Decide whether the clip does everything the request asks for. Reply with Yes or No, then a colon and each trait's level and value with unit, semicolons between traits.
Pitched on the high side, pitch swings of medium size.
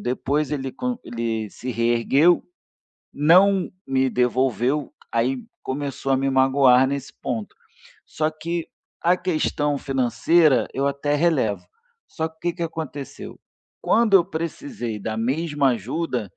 No: medium, 140 Hz; average, 4.5 semitones